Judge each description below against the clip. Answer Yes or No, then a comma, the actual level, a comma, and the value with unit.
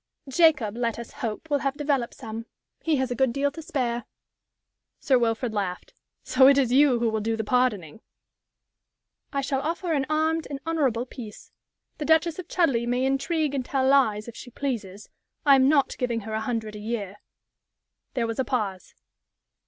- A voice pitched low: No, very high, 255 Hz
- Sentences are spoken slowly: No, average, 185 wpm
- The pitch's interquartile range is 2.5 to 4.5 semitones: Yes, average, 3.8 semitones